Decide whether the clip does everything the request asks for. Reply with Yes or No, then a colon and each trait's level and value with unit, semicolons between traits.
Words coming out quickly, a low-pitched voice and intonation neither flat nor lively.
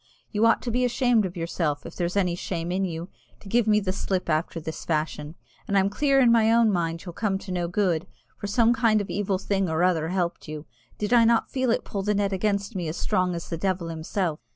No: fast, 245 wpm; high, 190 Hz; average, 3.9 semitones